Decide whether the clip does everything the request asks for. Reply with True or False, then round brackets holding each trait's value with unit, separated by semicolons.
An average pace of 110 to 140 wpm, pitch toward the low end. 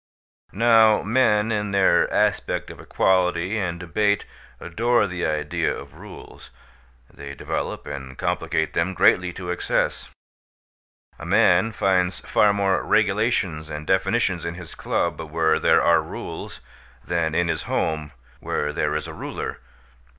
True (135 wpm; 90 Hz)